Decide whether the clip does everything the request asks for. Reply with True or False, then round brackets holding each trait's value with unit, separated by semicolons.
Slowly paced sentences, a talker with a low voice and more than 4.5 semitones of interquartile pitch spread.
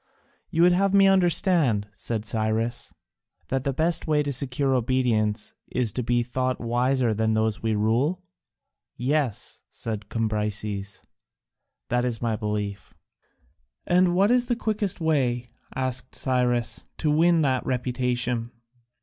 True (130 wpm; 125 Hz; 5.3 semitones)